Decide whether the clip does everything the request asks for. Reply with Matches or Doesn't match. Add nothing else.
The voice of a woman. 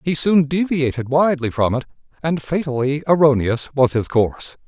Doesn't match